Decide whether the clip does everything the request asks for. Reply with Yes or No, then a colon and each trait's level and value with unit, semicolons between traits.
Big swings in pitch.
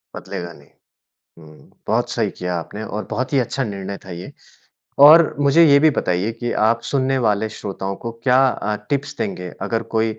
Yes: wide, 5.7 semitones